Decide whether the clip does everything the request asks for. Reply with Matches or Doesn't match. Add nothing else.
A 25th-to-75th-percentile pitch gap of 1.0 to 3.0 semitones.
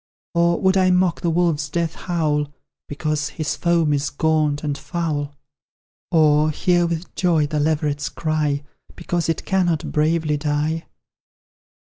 Matches